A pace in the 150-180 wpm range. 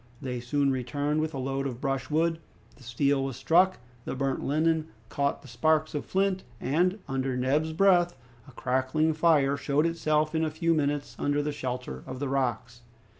Yes: average, 175 wpm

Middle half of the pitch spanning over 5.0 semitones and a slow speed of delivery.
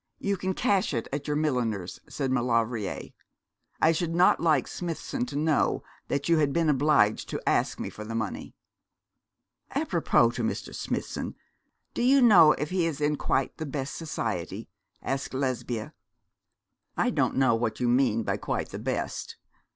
No: wide, 5.5 semitones; average, 165 wpm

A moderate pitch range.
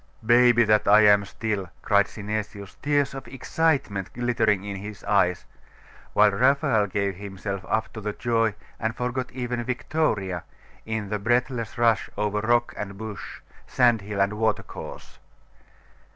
Yes: average, 3.0 semitones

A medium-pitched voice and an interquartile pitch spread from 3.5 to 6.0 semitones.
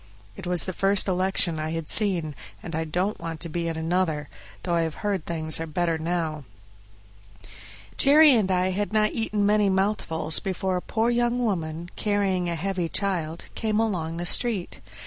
Yes: medium, 180 Hz; average, 3.8 semitones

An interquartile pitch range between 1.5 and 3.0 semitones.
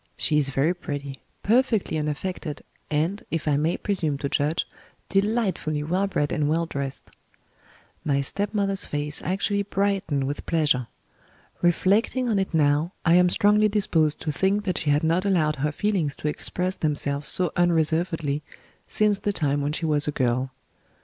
No: average, 4.8 semitones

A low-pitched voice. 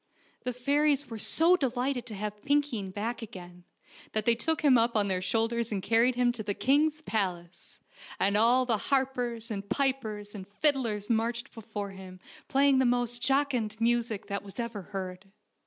No: high, 230 Hz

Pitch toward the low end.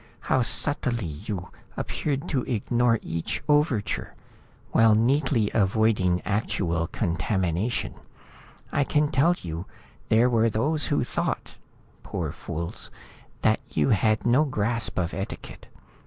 Yes: low, 110 Hz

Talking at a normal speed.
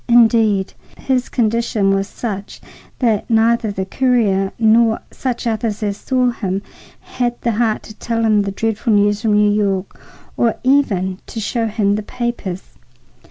Yes: average, 155 wpm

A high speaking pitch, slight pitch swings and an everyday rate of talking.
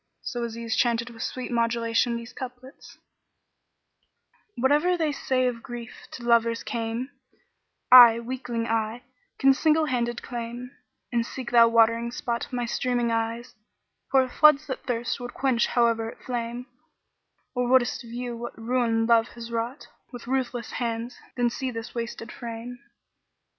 Yes: high, 240 Hz; narrow, 1.5 semitones; average, 150 wpm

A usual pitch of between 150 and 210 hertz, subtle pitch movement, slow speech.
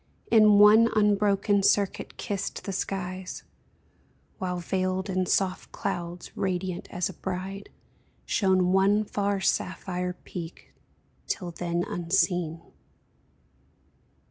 Yes: high, 190 Hz; narrow, 1.9 semitones; slow, 100 wpm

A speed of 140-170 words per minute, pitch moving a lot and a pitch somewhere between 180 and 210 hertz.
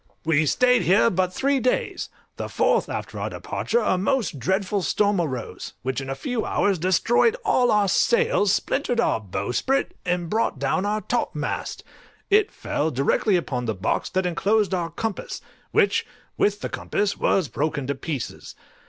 Yes: average, 160 wpm; wide, 7.1 semitones; high, 190 Hz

